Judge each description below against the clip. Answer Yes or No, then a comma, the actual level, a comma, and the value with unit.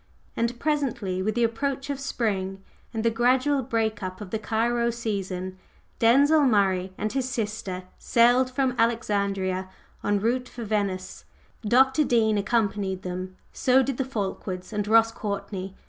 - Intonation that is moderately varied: Yes, average, 4.0 semitones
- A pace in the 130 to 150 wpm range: Yes, average, 145 wpm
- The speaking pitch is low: No, high, 225 Hz